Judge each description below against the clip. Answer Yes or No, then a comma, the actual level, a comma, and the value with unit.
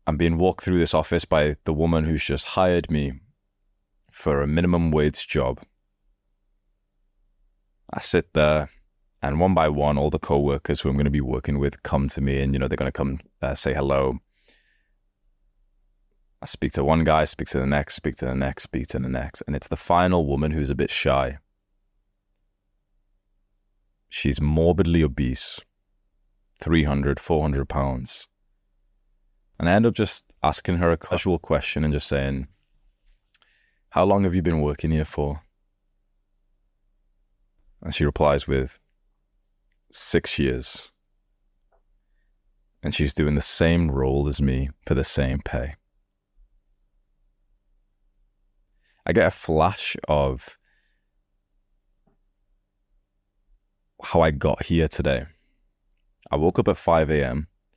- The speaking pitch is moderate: No, very low, 90 Hz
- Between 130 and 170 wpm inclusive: Yes, average, 140 wpm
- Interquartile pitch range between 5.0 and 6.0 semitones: Yes, wide, 5.4 semitones